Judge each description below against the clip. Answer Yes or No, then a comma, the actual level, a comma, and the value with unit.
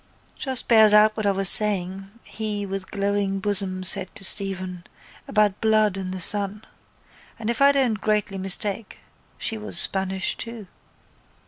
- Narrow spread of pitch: Yes, narrow, 2.0 semitones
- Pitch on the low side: No, high, 205 Hz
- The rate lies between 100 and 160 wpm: Yes, average, 150 wpm